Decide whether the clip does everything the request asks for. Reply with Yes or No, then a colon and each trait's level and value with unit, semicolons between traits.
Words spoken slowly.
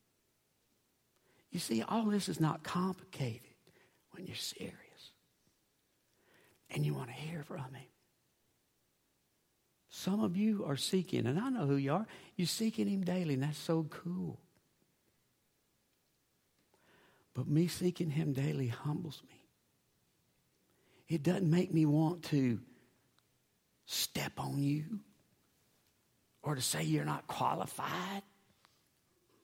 Yes: slow, 120 wpm